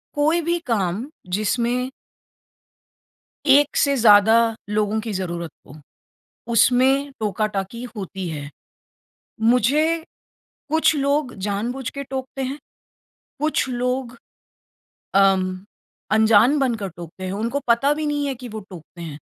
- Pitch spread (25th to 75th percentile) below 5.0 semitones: No, wide, 5.5 semitones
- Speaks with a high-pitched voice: Yes, high, 235 Hz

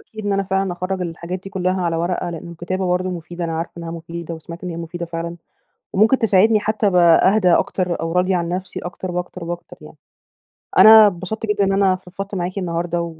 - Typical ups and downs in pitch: No, narrow, 2.1 semitones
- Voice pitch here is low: No, medium, 180 Hz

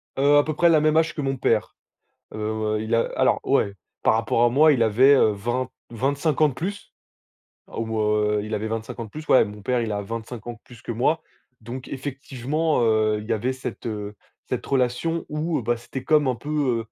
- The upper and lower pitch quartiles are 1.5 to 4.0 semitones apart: No, average, 4.6 semitones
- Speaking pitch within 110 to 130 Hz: Yes, low, 125 Hz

